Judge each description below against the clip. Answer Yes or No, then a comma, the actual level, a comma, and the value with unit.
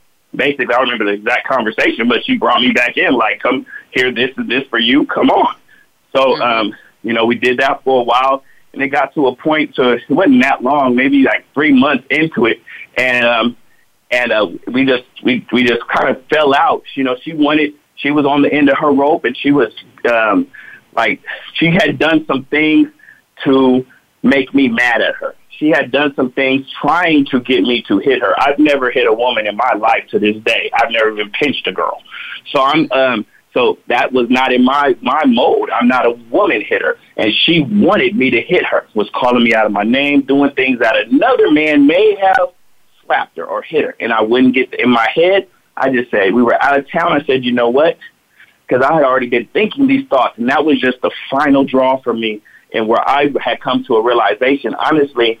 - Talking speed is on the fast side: Yes, fast, 225 wpm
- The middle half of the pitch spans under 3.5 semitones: No, average, 4.3 semitones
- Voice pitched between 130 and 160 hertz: Yes, low, 135 Hz